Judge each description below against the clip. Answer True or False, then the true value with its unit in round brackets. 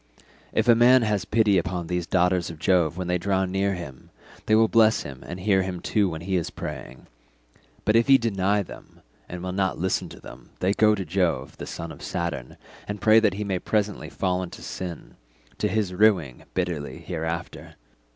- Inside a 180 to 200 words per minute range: True (195 wpm)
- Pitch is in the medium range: False (95 Hz)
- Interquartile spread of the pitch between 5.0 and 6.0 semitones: False (3.4 semitones)